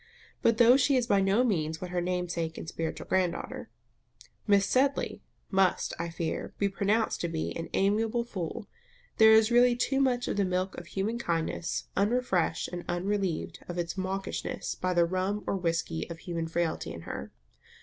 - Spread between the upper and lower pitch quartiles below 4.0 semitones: No, average, 4.5 semitones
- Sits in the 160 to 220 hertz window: Yes, high, 190 Hz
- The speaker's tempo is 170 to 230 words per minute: Yes, average, 180 wpm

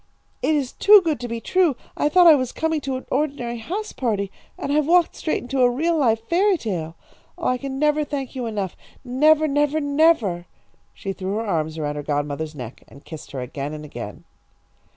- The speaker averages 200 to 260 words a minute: Yes, fast, 205 wpm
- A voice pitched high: Yes, very high, 255 Hz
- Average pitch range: No, wide, 8.3 semitones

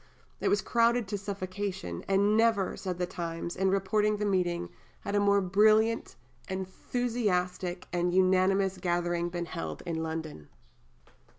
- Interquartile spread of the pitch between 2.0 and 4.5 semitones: Yes, average, 2.7 semitones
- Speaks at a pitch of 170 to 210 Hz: Yes, high, 190 Hz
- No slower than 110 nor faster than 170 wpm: Yes, slow, 135 wpm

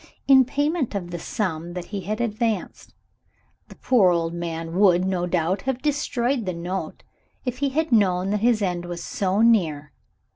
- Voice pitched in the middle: No, high, 195 Hz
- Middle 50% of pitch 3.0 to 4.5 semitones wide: No, wide, 5.4 semitones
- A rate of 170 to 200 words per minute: Yes, average, 175 wpm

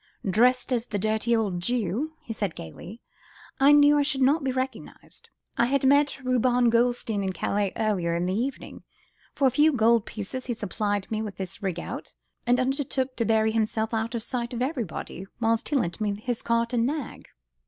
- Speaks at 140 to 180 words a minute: No, average, 195 wpm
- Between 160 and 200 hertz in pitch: No, high, 235 Hz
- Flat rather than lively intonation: No, average, 3.4 semitones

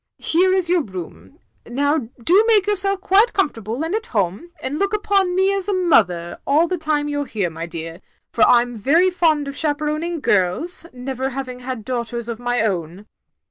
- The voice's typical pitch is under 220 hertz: No, very high, 285 Hz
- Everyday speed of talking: Yes, average, 190 wpm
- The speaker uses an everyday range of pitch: No, wide, 7.8 semitones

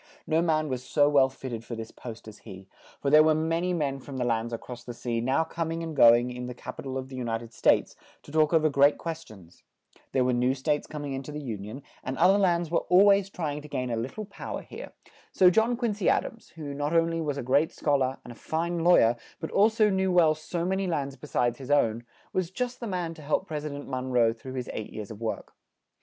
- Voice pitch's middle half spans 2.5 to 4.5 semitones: No, average, 5.0 semitones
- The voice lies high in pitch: No, medium, 145 Hz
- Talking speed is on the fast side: Yes, fast, 295 wpm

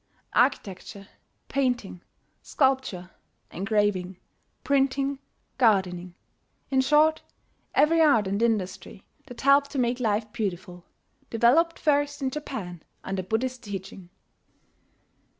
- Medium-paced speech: No, slow, 95 wpm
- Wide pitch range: Yes, wide, 6.2 semitones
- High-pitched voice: Yes, high, 230 Hz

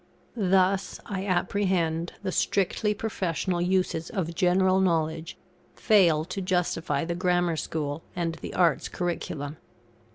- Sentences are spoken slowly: Yes, slow, 120 wpm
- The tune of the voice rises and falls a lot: No, narrow, 2.5 semitones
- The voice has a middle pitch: Yes, medium, 180 Hz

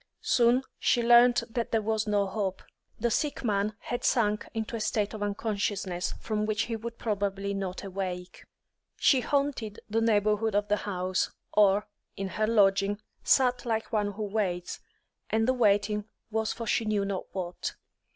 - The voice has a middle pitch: No, high, 210 Hz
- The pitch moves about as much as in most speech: No, narrow, 2.2 semitones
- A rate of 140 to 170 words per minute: Yes, average, 165 wpm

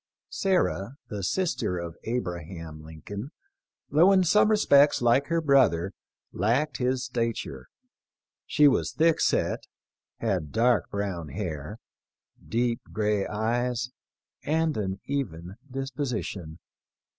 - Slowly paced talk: Yes, slow, 110 wpm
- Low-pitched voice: Yes, low, 115 Hz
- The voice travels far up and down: Yes, wide, 6.7 semitones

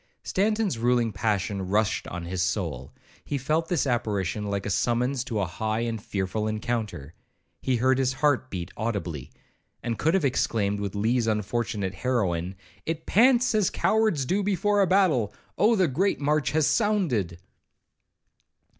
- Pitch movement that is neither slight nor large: No, wide, 7.8 semitones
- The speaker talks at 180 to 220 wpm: No, average, 150 wpm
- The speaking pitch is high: No, low, 115 Hz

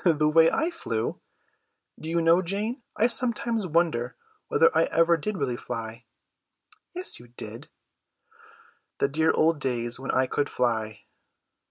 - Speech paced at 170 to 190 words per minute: No, average, 145 wpm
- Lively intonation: Yes, wide, 8.6 semitones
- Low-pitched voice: No, medium, 160 Hz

